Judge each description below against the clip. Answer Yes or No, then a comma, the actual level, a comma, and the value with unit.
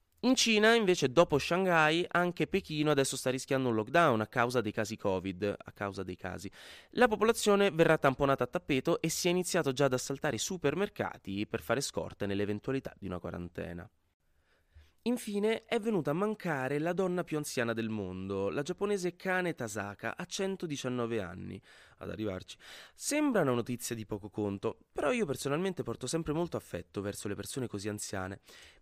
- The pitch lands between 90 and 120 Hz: No, low, 130 Hz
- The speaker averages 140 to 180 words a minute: Yes, fast, 170 wpm